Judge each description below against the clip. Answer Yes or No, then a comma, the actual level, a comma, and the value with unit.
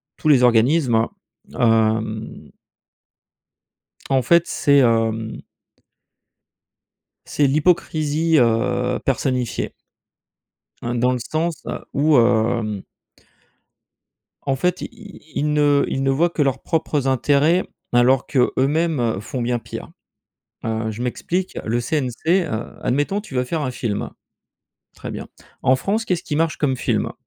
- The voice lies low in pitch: Yes, low, 130 Hz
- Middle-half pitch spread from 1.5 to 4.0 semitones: No, average, 4.7 semitones